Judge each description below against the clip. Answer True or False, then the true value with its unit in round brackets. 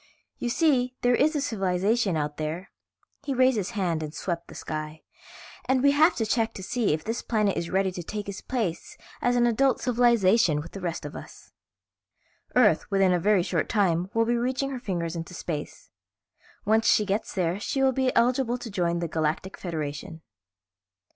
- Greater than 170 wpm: True (190 wpm)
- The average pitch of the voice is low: False (205 Hz)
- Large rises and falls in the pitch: True (6.2 semitones)